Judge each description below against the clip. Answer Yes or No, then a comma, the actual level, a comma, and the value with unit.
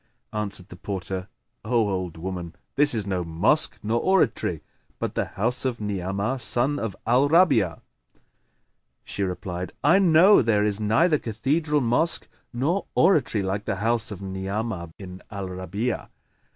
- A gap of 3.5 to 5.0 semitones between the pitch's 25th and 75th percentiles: No, wide, 5.4 semitones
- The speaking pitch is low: Yes, low, 105 Hz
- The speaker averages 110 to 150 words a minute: Yes, average, 145 wpm